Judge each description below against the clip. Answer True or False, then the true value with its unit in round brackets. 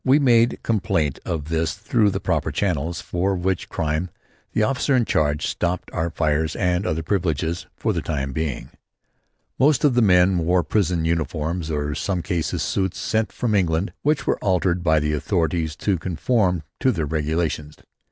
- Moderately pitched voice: False (85 Hz)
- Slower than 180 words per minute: True (170 wpm)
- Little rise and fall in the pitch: False (4.0 semitones)